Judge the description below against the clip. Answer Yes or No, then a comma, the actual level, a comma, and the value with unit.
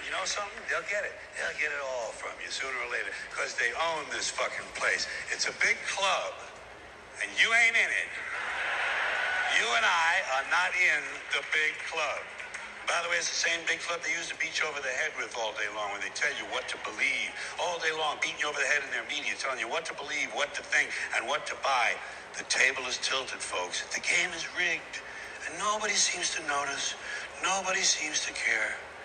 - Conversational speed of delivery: No, fast, 220 wpm